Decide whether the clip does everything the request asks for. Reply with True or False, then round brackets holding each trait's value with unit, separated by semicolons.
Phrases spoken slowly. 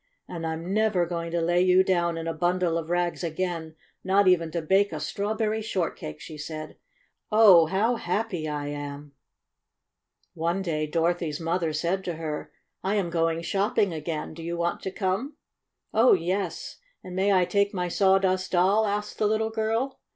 False (180 wpm)